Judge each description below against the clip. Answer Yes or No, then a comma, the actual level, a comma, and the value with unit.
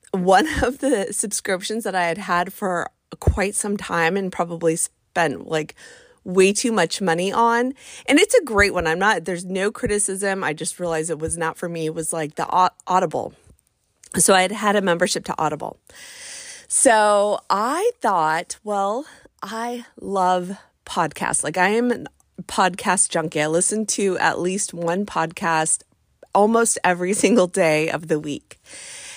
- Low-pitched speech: No, medium, 185 Hz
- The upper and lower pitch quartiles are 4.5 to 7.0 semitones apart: No, average, 3.5 semitones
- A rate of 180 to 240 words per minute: No, average, 165 wpm